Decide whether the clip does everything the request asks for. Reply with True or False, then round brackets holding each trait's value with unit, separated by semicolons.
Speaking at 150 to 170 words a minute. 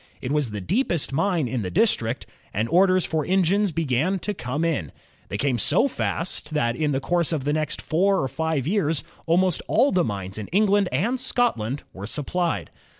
False (205 wpm)